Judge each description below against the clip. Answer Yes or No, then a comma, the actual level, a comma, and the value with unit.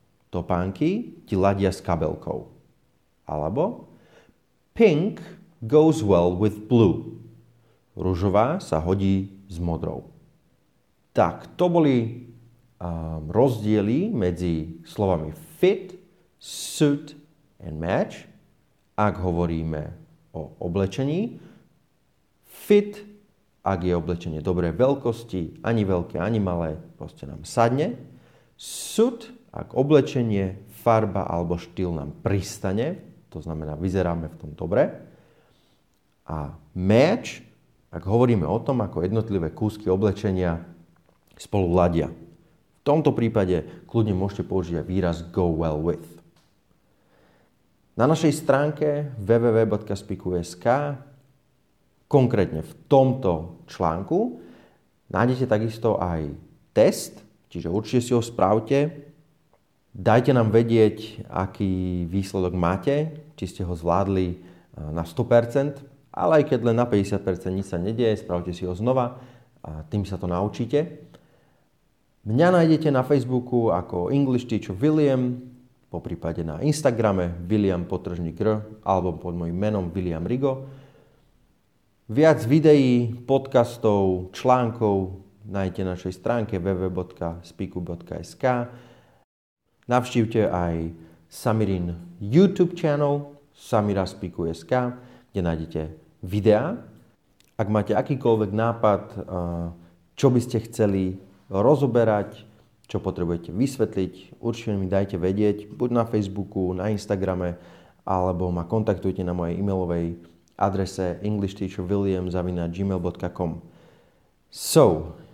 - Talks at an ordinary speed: No, slow, 100 wpm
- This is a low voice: Yes, low, 100 Hz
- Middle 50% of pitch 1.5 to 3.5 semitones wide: No, wide, 5.5 semitones